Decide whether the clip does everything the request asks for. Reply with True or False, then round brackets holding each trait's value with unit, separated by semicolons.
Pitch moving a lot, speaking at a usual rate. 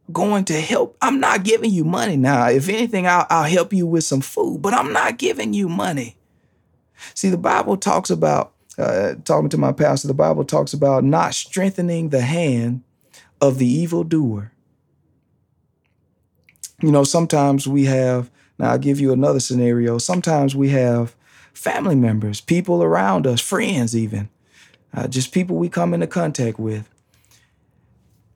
True (6.1 semitones; 160 wpm)